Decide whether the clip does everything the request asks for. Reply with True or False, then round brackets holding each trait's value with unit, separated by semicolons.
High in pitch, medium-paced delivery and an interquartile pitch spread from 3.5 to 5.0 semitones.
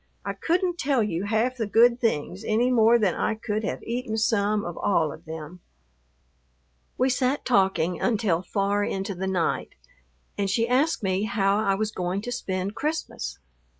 True (210 Hz; 170 wpm; 3.9 semitones)